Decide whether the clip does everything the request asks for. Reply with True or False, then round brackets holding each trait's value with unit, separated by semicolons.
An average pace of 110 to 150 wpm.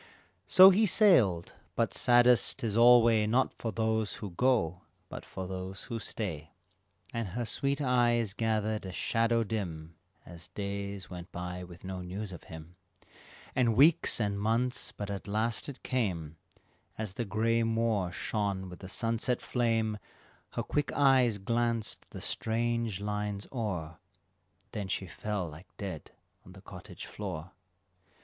True (145 wpm)